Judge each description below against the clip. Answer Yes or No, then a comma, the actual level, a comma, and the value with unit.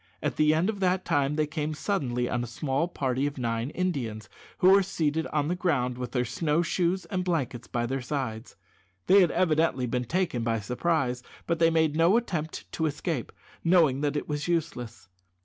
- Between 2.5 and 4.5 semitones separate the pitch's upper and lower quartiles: No, average, 5.3 semitones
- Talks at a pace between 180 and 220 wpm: Yes, average, 195 wpm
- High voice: No, medium, 150 Hz